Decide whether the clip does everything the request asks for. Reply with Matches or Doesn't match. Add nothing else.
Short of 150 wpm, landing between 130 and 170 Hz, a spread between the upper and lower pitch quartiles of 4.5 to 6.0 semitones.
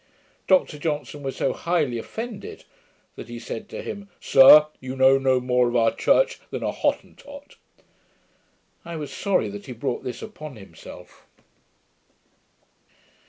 Matches